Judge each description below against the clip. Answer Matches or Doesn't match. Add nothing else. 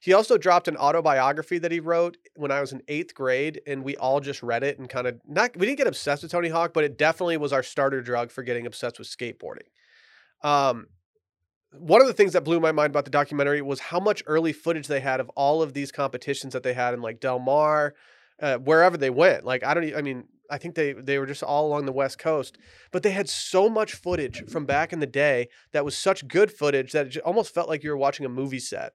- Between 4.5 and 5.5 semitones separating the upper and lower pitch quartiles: Doesn't match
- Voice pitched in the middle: Matches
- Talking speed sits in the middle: Doesn't match